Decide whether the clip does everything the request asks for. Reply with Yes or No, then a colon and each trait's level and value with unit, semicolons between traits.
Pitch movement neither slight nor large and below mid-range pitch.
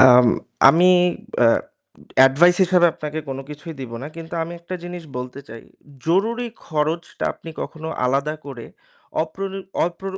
No: average, 4.5 semitones; medium, 160 Hz